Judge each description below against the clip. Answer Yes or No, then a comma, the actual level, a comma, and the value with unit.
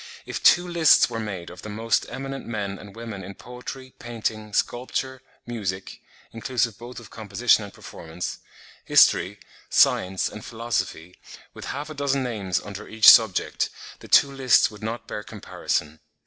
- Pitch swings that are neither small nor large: Yes, average, 3.7 semitones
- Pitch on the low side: Yes, low, 110 Hz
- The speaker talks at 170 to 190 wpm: No, average, 155 wpm